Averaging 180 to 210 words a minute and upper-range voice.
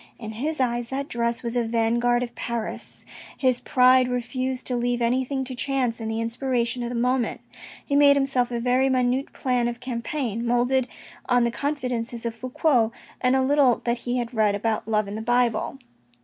Yes: average, 190 wpm; high, 245 Hz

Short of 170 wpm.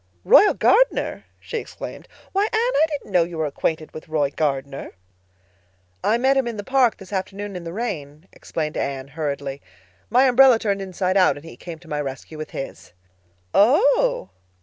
No: average, 175 wpm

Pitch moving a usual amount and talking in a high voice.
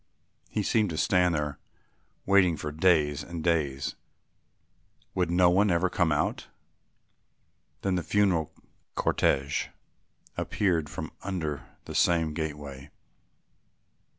No: average, 3.5 semitones; very low, 85 Hz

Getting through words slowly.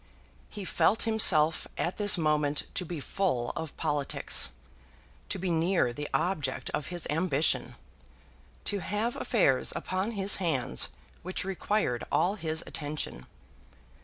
Yes: slow, 130 wpm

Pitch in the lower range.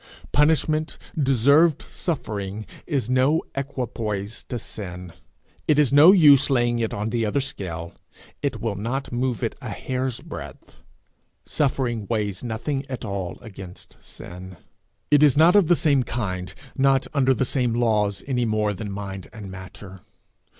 Yes: low, 120 Hz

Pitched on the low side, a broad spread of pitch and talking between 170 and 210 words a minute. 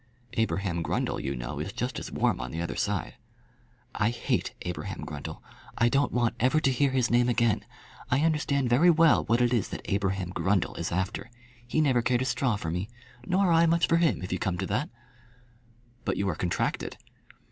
Yes: low, 120 Hz; wide, 6.4 semitones; average, 200 wpm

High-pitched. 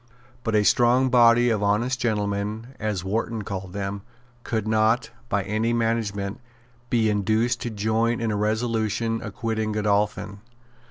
No: low, 110 Hz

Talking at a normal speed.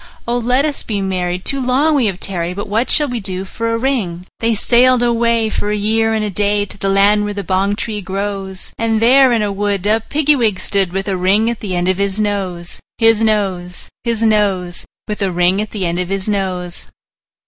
No: fast, 225 wpm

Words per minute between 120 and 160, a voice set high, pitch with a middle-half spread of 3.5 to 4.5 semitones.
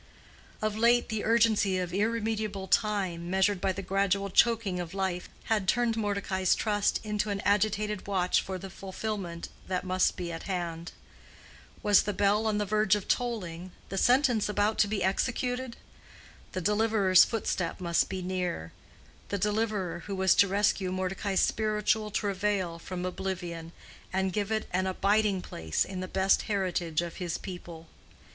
No: average, 155 wpm; high, 195 Hz; narrow, 2.5 semitones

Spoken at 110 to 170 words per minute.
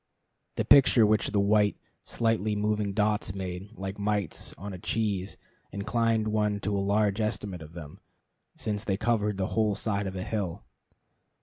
Yes: average, 165 wpm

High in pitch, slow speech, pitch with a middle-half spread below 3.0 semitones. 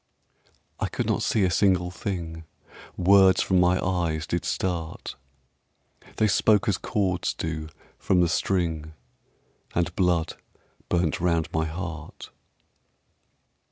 No: very low, 90 Hz; slow, 120 wpm; narrow, 2.4 semitones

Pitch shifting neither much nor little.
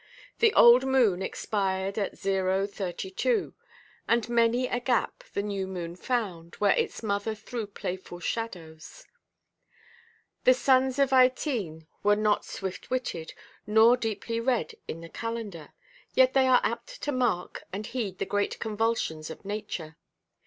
Yes: average, 4.6 semitones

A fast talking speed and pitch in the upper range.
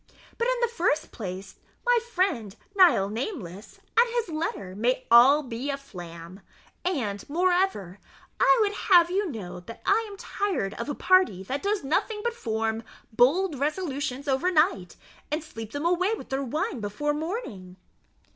No: average, 155 wpm; very high, 285 Hz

